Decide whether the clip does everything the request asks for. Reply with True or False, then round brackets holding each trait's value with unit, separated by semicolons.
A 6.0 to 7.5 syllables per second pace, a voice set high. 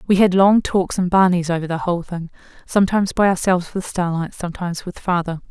False (6.3 syllables/s; 180 Hz)